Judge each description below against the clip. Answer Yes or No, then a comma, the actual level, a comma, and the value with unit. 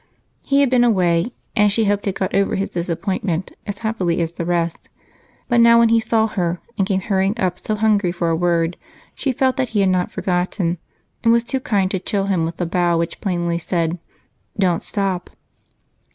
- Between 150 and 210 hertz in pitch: Yes, high, 190 Hz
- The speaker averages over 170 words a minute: Yes, average, 200 wpm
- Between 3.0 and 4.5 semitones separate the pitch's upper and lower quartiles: Yes, average, 4.1 semitones